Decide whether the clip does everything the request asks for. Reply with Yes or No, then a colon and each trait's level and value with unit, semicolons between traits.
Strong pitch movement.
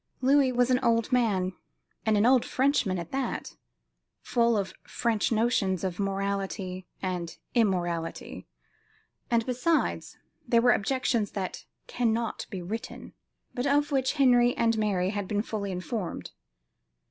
No: average, 4.3 semitones